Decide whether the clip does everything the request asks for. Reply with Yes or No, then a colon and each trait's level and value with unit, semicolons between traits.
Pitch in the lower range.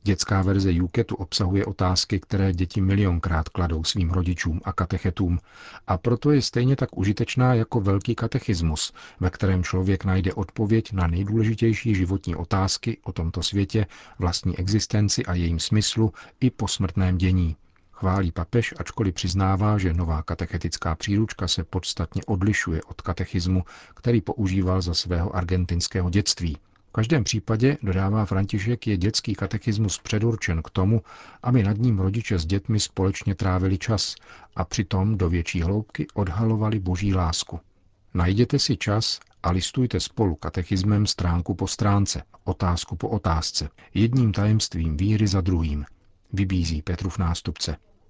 Yes: very low, 95 Hz